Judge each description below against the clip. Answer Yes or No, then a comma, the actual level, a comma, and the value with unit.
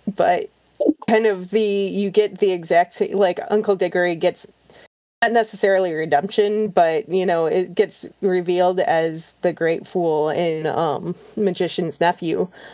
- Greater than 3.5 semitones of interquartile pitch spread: No, average, 3.1 semitones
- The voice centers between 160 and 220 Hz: Yes, medium, 185 Hz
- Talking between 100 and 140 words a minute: Yes, slow, 135 wpm